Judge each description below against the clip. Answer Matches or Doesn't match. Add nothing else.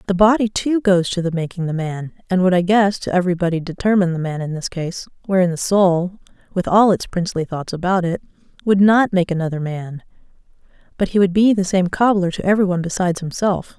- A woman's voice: Matches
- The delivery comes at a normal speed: Doesn't match